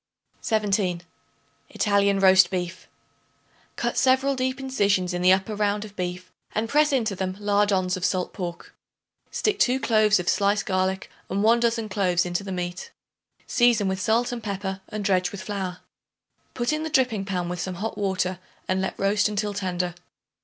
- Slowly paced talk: No, average, 170 wpm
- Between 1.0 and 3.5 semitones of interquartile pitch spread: Yes, average, 2.8 semitones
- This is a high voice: Yes, high, 200 Hz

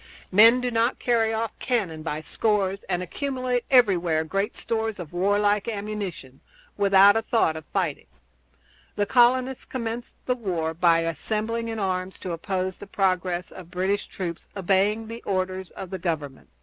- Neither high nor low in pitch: No, high, 195 Hz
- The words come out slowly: No, average, 155 wpm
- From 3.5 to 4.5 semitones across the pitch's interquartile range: Yes, average, 4.1 semitones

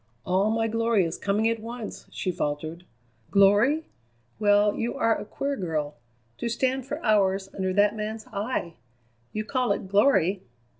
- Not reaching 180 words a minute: Yes, average, 155 wpm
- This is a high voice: Yes, high, 210 Hz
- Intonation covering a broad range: No, average, 3.2 semitones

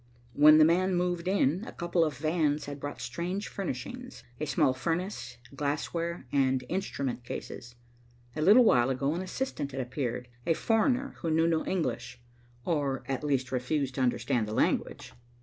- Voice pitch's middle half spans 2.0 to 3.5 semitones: No, average, 5.1 semitones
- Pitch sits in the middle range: Yes, medium, 150 Hz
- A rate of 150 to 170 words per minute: Yes, average, 165 wpm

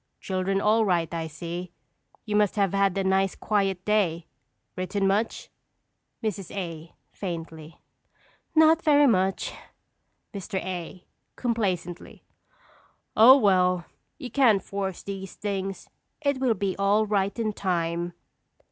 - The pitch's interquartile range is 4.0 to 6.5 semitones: No, average, 2.9 semitones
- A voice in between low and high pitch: No, high, 195 Hz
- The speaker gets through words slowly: Yes, slow, 120 wpm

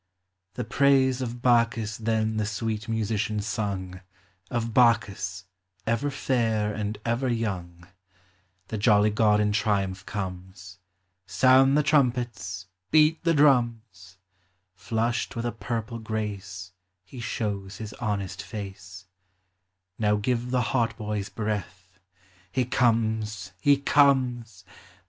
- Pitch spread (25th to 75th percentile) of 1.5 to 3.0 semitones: No, average, 3.4 semitones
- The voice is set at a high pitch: No, low, 110 Hz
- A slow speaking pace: Yes, slow, 115 wpm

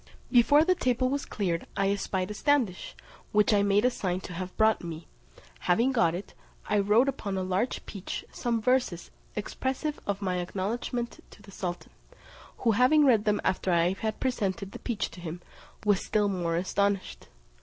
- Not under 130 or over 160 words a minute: No, average, 175 wpm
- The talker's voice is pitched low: No, high, 205 Hz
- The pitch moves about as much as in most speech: Yes, average, 4.4 semitones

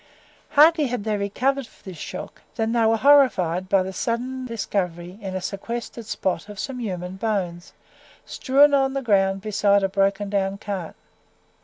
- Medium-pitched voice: No, high, 205 Hz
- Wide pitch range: No, average, 4.3 semitones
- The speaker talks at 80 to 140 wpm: No, average, 160 wpm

